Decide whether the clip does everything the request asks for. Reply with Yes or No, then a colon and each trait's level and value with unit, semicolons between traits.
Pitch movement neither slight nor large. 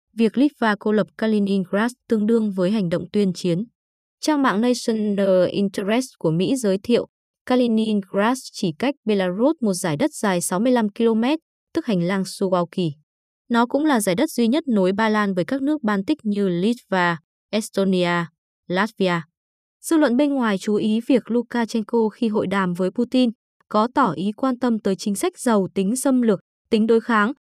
Yes: average, 3.8 semitones